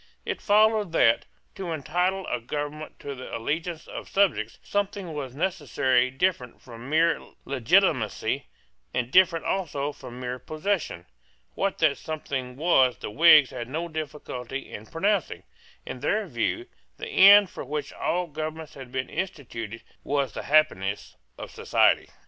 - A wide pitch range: Yes, wide, 5.8 semitones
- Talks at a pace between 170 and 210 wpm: No, average, 145 wpm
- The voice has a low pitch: No, medium, 150 Hz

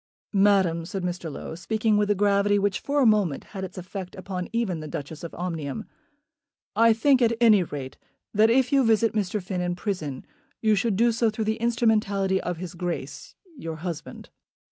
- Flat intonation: No, average, 3.9 semitones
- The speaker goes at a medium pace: Yes, average, 190 wpm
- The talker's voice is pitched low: No, high, 200 Hz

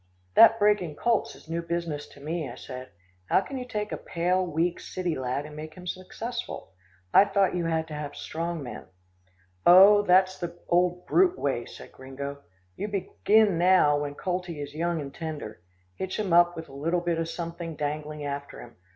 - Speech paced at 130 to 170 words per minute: No, average, 190 wpm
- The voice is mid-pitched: Yes, medium, 170 Hz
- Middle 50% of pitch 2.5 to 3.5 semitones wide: No, average, 3.9 semitones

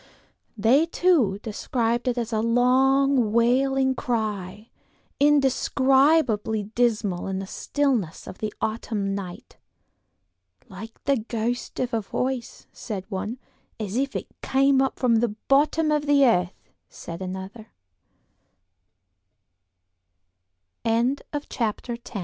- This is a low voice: No, high, 235 Hz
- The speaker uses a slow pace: Yes, slow, 105 wpm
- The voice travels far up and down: No, average, 4.3 semitones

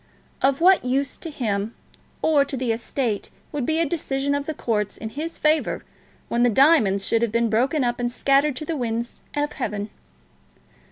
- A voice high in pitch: Yes, very high, 260 Hz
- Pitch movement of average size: Yes, average, 4.3 semitones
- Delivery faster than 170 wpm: Yes, average, 185 wpm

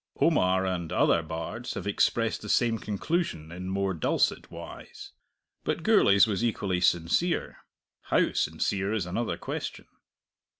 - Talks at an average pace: No, slow, 130 wpm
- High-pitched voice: No, very low, 95 Hz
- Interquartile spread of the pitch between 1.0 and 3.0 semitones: No, average, 4.0 semitones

